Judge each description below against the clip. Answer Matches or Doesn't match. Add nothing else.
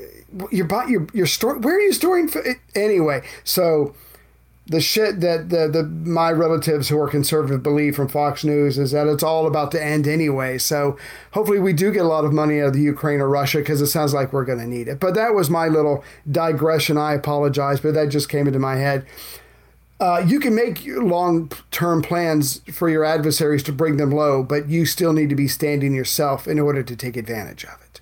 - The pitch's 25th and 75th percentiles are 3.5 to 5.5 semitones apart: Doesn't match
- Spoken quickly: Matches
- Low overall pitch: Doesn't match